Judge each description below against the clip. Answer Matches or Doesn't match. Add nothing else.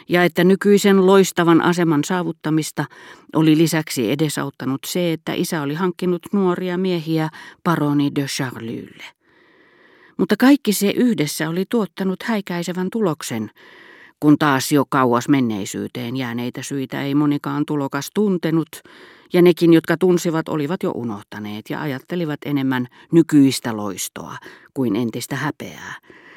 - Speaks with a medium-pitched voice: Matches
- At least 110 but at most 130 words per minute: Matches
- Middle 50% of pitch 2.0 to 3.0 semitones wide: Doesn't match